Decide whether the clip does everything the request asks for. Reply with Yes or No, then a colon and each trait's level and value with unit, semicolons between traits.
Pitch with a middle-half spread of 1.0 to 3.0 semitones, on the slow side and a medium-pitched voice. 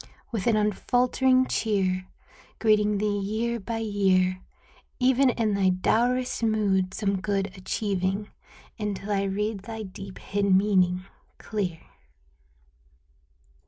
No: narrow, 2.5 semitones; slow, 110 wpm; high, 205 Hz